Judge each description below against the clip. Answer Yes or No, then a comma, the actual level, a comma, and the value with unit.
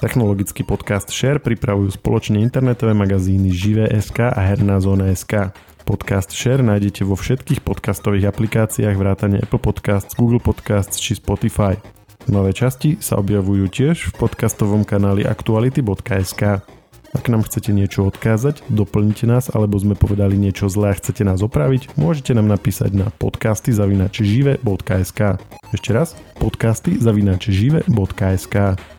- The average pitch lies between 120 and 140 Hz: No, low, 105 Hz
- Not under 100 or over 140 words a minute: Yes, average, 120 wpm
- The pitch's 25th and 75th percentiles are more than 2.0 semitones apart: Yes, average, 2.9 semitones